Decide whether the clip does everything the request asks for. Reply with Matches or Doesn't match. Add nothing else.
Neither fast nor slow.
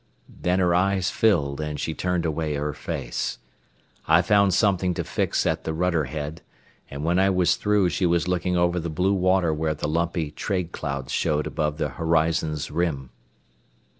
Matches